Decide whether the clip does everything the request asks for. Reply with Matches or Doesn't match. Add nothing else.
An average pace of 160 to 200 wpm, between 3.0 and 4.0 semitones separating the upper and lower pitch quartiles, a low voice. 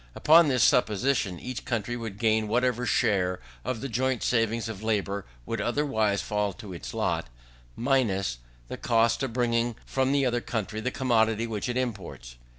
Matches